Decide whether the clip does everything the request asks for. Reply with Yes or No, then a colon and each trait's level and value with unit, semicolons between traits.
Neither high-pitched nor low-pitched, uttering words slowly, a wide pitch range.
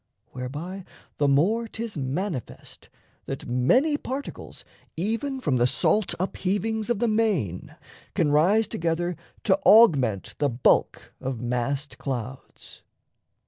Yes: medium, 170 Hz; slow, 115 wpm; wide, 8.6 semitones